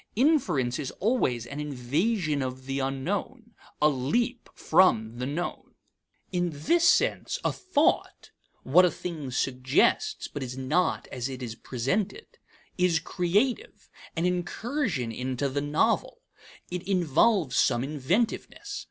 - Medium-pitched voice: Yes, medium, 150 Hz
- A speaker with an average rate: No, slow, 125 wpm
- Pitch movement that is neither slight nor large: No, wide, 7.4 semitones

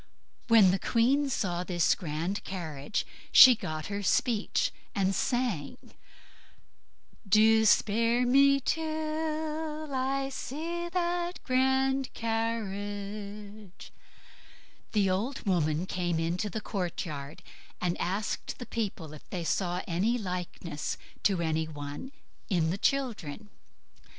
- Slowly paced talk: Yes, slow, 110 wpm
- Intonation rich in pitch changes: Yes, wide, 6.8 semitones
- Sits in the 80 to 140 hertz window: No, high, 210 Hz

